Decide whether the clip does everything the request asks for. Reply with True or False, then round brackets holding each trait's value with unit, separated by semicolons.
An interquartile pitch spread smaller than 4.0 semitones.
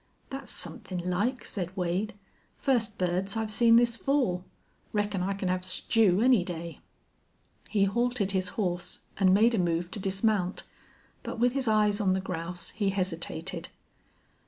True (3.6 semitones)